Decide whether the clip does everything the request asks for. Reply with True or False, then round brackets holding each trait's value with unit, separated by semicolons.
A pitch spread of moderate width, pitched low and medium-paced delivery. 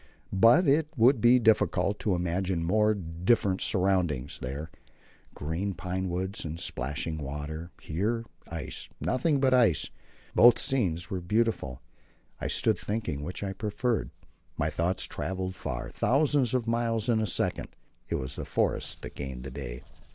False (6.1 semitones; 95 Hz; 150 wpm)